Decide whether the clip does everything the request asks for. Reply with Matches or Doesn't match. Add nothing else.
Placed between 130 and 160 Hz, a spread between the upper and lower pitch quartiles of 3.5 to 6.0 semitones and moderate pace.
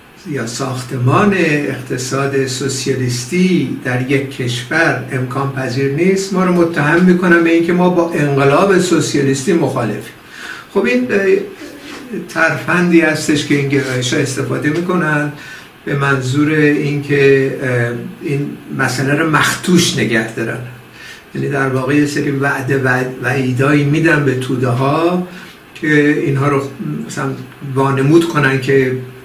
Matches